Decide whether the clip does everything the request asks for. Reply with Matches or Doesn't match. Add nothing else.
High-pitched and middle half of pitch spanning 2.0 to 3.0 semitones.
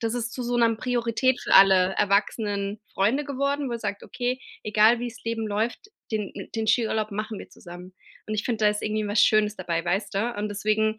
Matches